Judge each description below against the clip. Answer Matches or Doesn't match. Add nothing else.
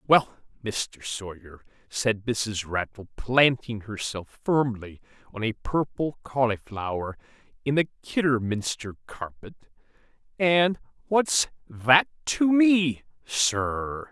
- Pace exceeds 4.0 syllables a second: Doesn't match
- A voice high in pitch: Doesn't match